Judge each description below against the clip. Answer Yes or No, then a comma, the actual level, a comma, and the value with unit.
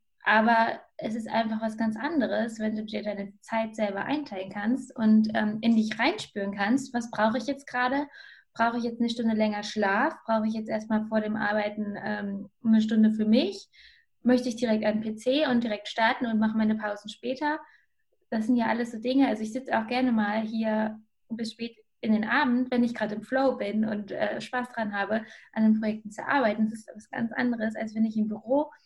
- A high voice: Yes, high, 225 Hz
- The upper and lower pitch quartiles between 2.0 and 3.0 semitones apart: Yes, narrow, 2.6 semitones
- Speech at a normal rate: No, fast, 210 wpm